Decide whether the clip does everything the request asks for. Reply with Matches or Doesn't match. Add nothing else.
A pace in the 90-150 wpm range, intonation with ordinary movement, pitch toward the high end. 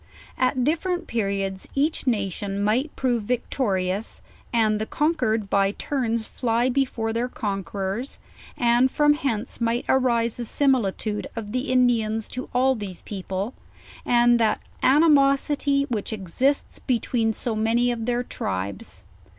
Matches